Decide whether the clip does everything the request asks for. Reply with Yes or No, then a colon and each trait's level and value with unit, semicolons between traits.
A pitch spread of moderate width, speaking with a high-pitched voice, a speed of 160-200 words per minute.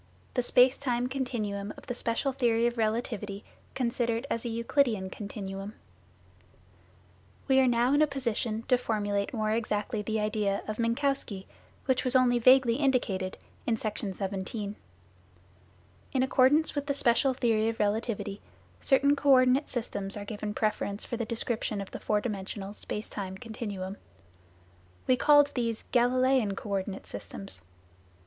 No: average, 3.6 semitones; high, 230 Hz; average, 150 wpm